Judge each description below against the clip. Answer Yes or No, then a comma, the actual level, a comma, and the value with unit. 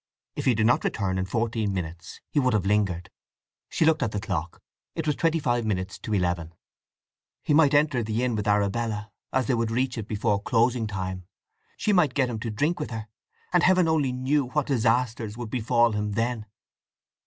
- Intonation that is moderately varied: Yes, average, 3.9 semitones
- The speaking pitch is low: Yes, low, 115 Hz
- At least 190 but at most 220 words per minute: Yes, average, 200 wpm